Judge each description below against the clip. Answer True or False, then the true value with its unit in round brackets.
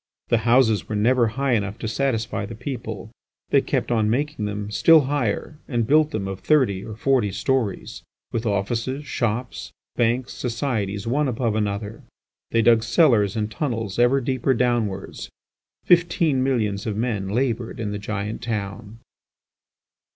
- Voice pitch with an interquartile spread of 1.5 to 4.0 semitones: True (3.7 semitones)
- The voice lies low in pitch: True (115 Hz)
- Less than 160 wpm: True (150 wpm)